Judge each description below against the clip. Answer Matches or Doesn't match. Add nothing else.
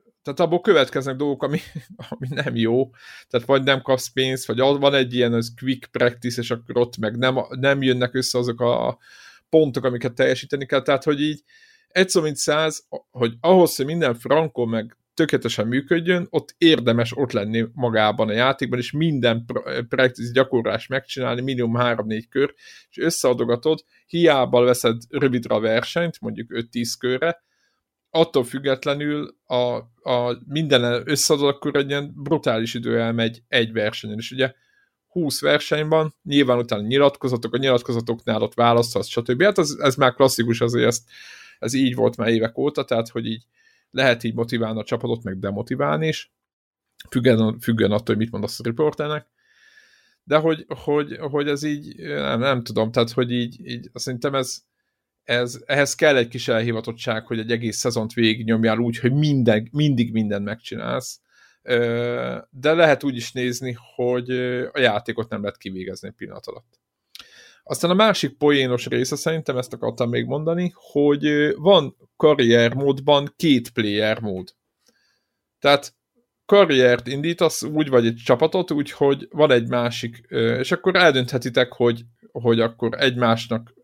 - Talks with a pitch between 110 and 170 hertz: Matches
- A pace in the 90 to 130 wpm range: Doesn't match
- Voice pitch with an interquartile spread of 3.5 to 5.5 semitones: Matches